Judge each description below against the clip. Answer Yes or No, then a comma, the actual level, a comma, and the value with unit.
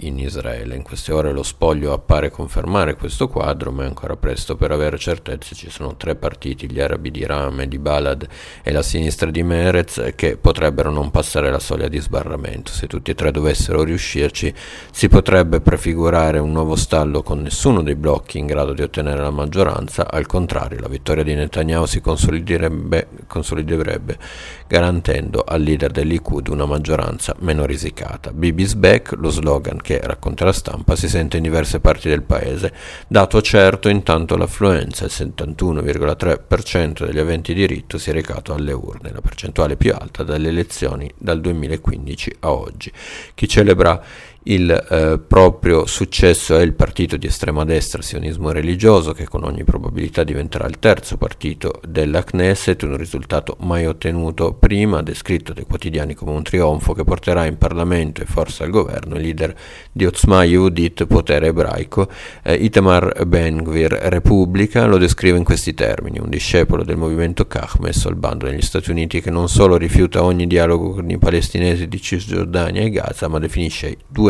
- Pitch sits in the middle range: No, very low, 80 Hz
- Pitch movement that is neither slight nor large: Yes, average, 3.1 semitones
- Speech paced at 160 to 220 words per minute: Yes, average, 165 wpm